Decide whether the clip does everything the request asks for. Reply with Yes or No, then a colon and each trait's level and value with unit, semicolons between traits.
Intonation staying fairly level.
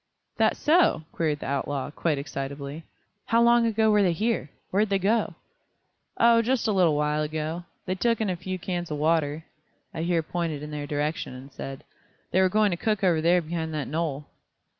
No: average, 5.1 semitones